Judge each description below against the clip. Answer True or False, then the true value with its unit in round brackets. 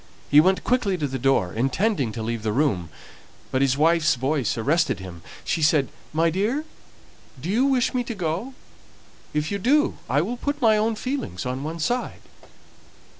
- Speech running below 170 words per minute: False (175 wpm)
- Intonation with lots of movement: True (8.9 semitones)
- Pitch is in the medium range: True (160 Hz)